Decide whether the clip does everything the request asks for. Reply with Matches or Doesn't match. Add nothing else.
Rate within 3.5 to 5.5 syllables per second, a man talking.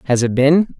Matches